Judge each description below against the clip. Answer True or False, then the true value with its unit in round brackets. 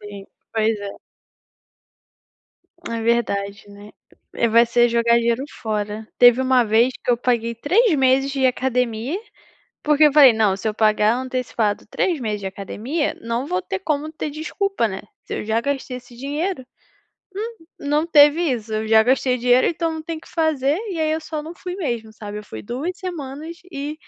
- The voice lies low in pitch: False (250 Hz)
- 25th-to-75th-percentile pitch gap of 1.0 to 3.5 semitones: False (5.3 semitones)